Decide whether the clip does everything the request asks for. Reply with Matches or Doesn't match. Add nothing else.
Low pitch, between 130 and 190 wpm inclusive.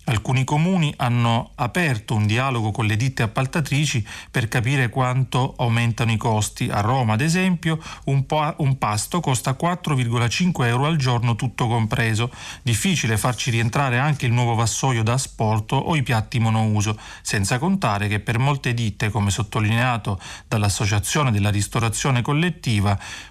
Matches